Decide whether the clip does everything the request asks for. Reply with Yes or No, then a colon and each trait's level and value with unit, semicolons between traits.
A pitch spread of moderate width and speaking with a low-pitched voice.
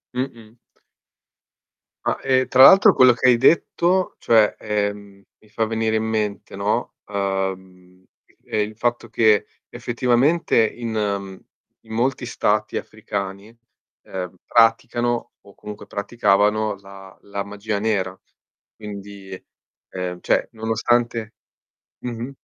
Yes: average, 3.0 semitones; low, 110 Hz